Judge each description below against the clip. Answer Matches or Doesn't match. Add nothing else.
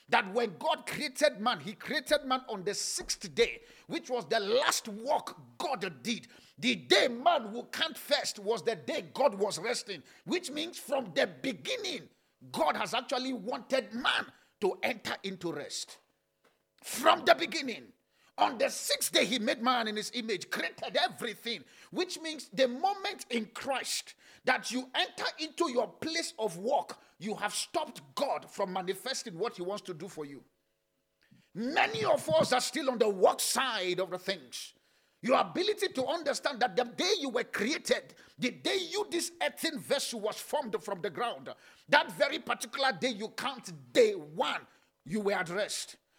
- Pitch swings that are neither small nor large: Doesn't match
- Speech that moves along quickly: Doesn't match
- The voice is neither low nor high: Doesn't match